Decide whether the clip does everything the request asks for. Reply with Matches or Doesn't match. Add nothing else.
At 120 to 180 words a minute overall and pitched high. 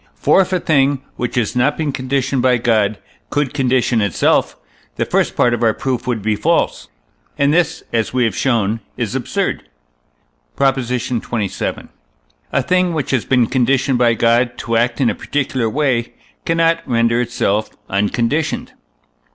Doesn't match